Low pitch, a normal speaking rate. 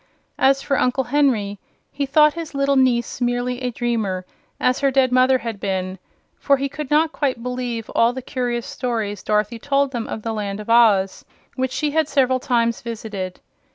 No: very high, 250 Hz; average, 185 wpm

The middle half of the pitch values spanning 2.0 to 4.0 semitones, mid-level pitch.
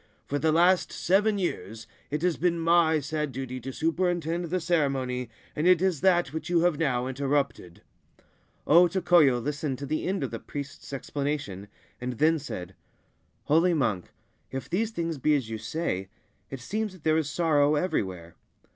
No: average, 4.6 semitones; medium, 150 Hz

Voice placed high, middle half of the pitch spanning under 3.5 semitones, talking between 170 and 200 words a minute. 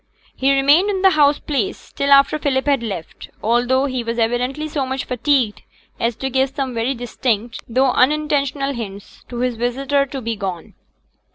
Yes: very high, 265 Hz; average, 3.0 semitones; average, 175 wpm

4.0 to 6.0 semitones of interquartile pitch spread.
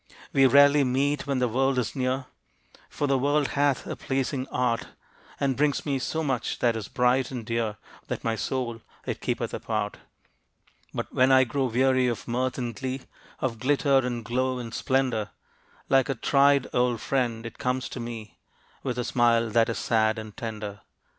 No: narrow, 2.5 semitones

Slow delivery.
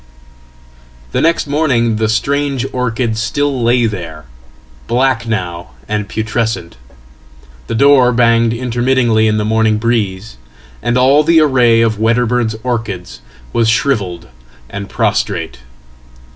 Yes: slow, 110 wpm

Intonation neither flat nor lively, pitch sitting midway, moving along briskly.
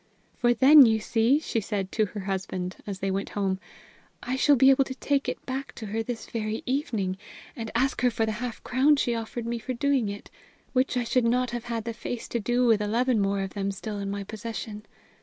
No: average, 3.4 semitones; high, 230 Hz; fast, 230 wpm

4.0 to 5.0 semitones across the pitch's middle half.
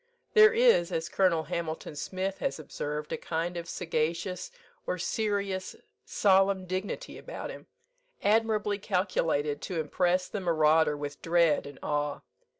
No: average, 3.6 semitones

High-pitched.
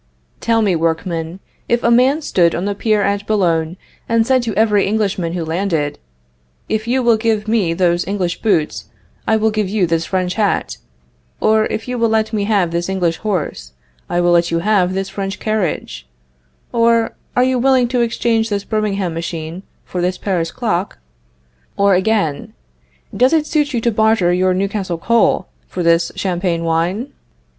Yes: high, 200 Hz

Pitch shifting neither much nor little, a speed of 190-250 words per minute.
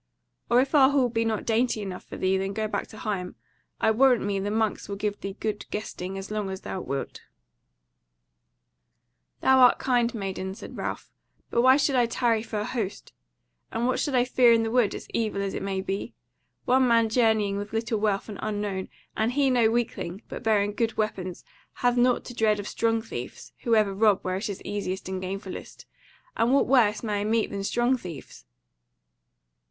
Yes: average, 3.2 semitones; average, 200 wpm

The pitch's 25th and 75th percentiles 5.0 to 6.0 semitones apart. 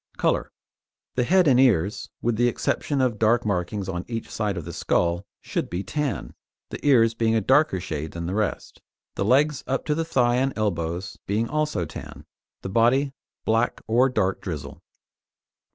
Yes: wide, 5.6 semitones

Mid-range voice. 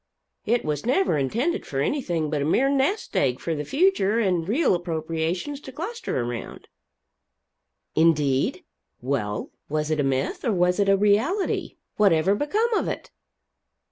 Yes: medium, 180 Hz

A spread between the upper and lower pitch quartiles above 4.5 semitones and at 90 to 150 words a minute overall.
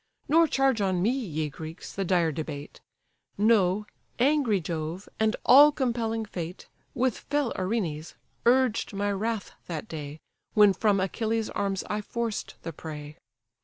Yes: wide, 5.6 semitones; average, 140 wpm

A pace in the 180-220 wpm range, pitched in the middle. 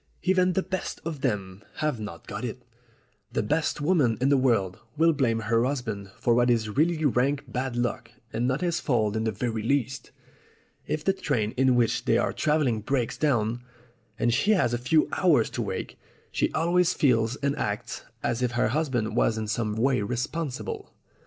No: average, 185 wpm; low, 125 Hz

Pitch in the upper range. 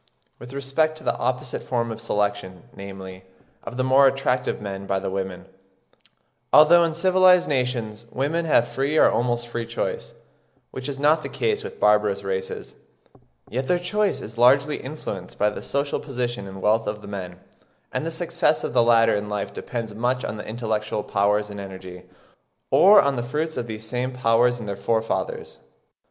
No: low, 120 Hz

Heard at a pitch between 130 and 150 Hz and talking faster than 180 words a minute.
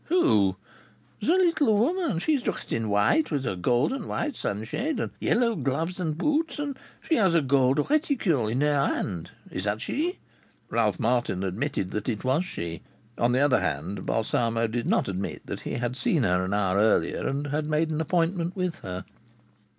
Yes: medium, 140 Hz; average, 190 wpm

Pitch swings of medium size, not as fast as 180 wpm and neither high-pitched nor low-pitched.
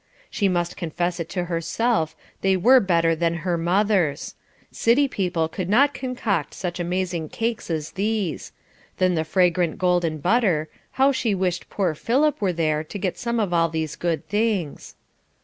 Yes: average, 3.9 semitones; average, 165 wpm; medium, 180 Hz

